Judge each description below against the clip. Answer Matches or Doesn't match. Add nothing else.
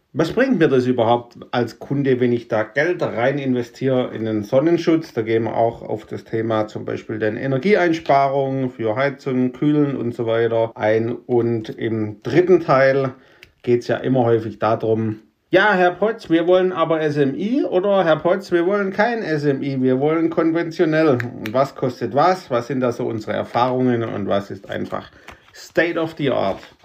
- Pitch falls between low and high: Doesn't match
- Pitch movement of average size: Doesn't match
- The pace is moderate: Matches